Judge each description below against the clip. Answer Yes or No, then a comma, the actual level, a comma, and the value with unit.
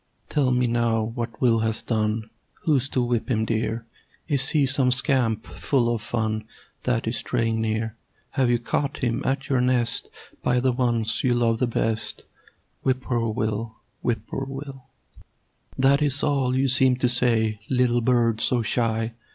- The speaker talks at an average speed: Yes, average, 165 wpm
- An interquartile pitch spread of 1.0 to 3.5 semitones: Yes, narrow, 2.4 semitones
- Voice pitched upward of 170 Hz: No, low, 120 Hz